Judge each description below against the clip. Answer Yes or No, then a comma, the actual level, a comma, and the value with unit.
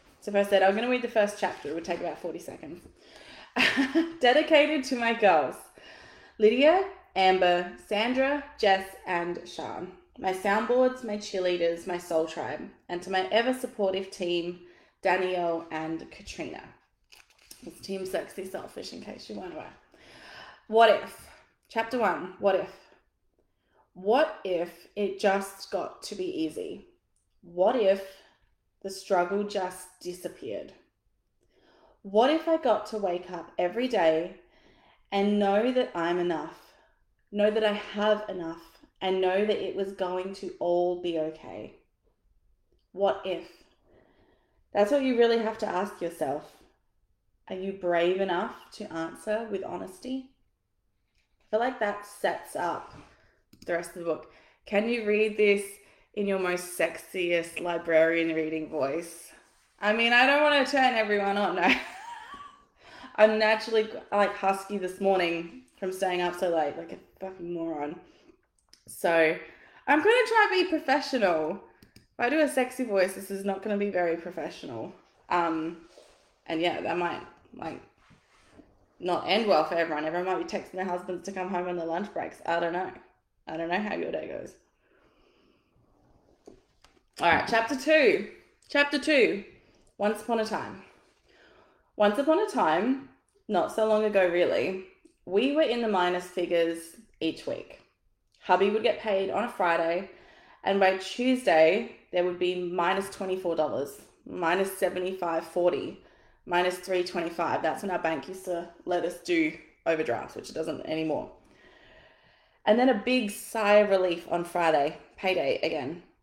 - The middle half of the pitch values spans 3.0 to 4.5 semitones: Yes, average, 4.1 semitones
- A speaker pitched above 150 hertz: Yes, high, 190 Hz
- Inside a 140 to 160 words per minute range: Yes, average, 150 wpm